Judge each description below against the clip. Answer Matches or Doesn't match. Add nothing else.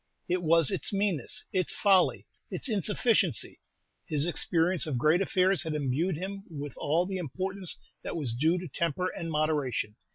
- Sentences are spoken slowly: Doesn't match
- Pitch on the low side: Doesn't match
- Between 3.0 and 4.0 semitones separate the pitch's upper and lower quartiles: Matches